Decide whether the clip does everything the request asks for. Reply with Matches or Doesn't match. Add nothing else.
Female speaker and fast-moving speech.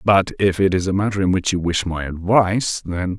Doesn't match